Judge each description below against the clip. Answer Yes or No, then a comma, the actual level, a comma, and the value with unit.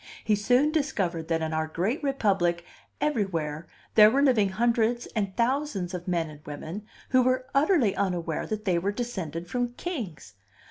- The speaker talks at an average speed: Yes, average, 165 wpm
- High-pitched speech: Yes, high, 205 Hz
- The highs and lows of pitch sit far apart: Yes, wide, 6.3 semitones